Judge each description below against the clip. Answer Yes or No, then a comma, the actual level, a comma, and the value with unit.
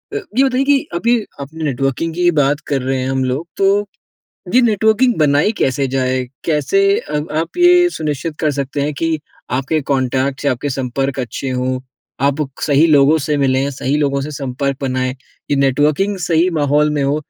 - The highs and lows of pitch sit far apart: No, average, 3.4 semitones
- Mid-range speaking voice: Yes, medium, 145 Hz